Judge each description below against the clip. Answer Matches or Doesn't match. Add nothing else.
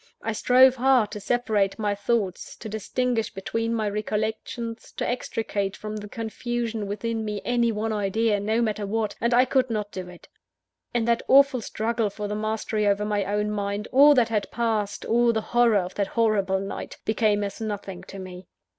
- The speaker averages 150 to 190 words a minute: Matches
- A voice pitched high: Matches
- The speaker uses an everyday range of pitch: Doesn't match